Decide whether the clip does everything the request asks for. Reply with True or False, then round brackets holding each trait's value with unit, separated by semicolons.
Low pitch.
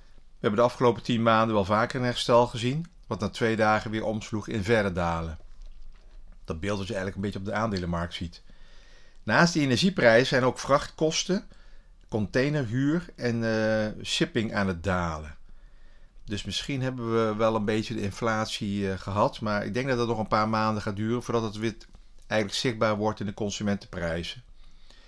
True (110 Hz)